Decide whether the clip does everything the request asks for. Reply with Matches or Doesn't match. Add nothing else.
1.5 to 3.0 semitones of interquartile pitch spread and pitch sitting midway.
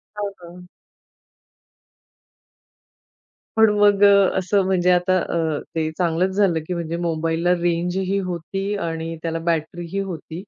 Matches